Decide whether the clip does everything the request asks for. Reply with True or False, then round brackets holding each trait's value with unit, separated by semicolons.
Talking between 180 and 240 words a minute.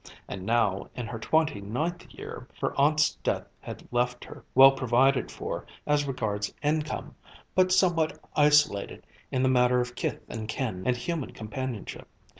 False (155 wpm)